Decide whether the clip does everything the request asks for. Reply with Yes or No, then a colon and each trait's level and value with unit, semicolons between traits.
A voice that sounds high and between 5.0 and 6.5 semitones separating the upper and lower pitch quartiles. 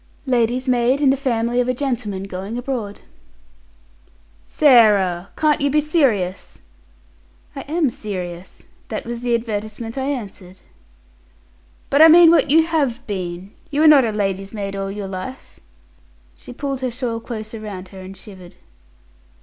Yes: high, 230 Hz; wide, 5.4 semitones